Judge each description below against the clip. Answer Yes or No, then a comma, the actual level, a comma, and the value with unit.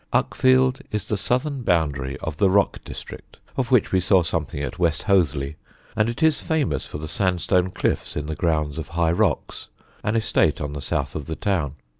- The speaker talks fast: Yes, fast, 215 wpm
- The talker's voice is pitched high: No, very low, 90 Hz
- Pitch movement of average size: No, wide, 5.9 semitones